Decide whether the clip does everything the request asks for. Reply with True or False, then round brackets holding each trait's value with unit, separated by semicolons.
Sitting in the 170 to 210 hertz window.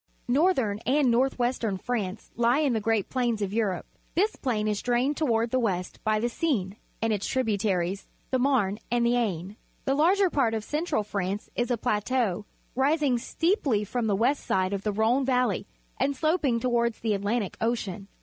False (235 Hz)